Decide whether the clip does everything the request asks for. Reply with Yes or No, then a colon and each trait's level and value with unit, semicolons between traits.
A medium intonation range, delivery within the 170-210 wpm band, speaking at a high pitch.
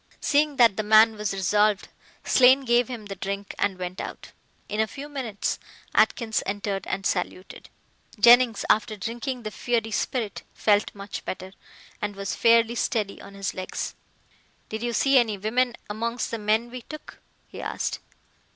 No: average, 3.2 semitones; average, 160 wpm; high, 220 Hz